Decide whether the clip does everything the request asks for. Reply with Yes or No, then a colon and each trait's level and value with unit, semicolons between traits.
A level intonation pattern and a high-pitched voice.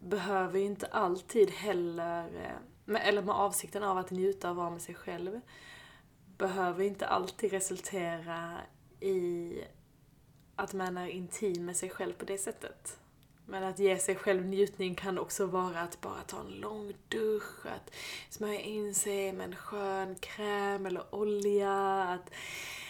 Yes: narrow, 1.8 semitones; high, 195 Hz